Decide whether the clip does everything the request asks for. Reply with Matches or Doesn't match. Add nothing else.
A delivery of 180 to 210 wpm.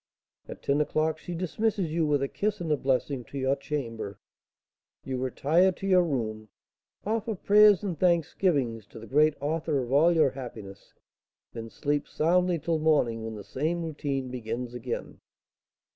Doesn't match